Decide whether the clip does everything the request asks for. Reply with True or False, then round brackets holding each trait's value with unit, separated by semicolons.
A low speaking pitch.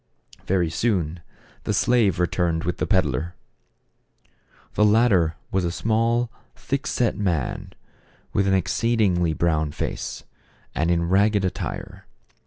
True (95 Hz)